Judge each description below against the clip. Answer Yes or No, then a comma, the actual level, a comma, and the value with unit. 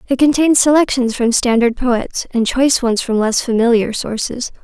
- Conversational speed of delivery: Yes, average, 170 wpm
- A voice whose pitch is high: Yes, high, 245 Hz